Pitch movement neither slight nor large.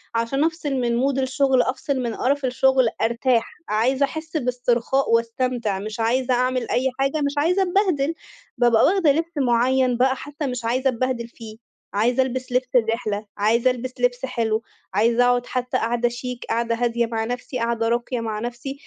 No: narrow, 2.2 semitones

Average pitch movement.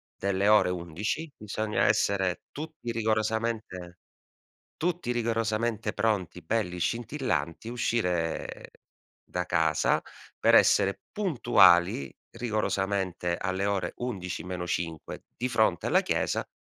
Yes: average, 4.5 semitones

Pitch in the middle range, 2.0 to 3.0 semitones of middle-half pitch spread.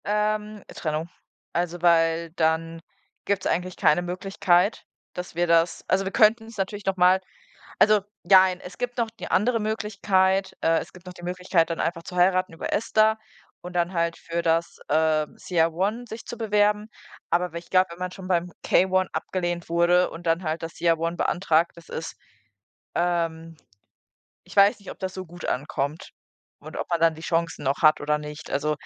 Yes: medium, 175 Hz; narrow, 2.6 semitones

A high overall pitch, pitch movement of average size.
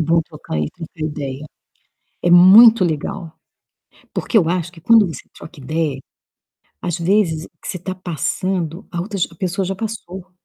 No: medium, 175 Hz; average, 3.1 semitones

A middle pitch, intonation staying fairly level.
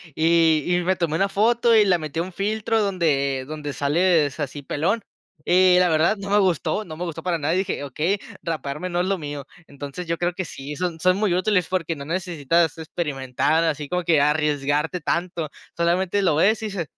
No: medium, 170 Hz; average, 3.7 semitones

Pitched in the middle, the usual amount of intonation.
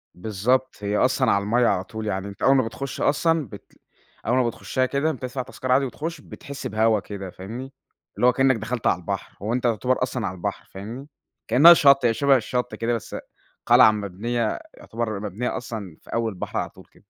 No: low, 120 Hz; average, 3.6 semitones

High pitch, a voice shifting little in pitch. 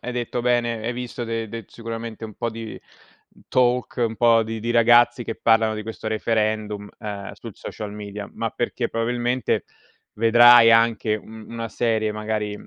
No: low, 115 Hz; narrow, 1.6 semitones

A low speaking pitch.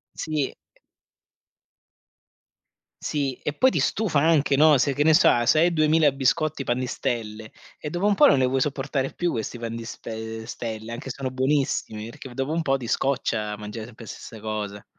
Yes: low, 130 Hz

